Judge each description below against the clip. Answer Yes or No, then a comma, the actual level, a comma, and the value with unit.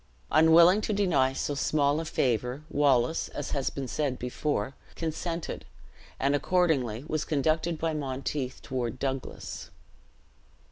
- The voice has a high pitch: No, medium, 145 Hz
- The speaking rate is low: Yes, slow, 125 wpm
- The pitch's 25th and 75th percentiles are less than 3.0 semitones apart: No, average, 3.6 semitones